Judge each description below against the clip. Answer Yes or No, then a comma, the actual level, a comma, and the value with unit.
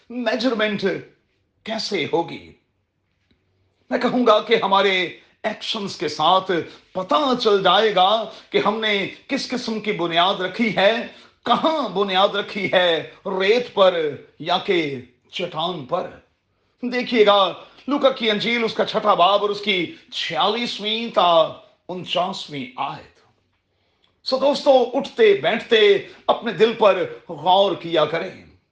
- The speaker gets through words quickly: No, average, 125 wpm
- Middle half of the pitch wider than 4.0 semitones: Yes, average, 4.5 semitones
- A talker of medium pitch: No, high, 210 Hz